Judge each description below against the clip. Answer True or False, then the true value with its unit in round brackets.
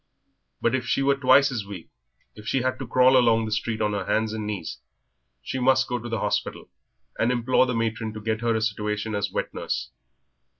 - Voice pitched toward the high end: False (115 Hz)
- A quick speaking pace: True (215 wpm)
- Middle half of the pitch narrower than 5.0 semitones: True (2.9 semitones)